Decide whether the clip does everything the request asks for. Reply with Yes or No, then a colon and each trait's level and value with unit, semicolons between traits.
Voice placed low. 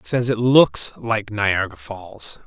Yes: low, 105 Hz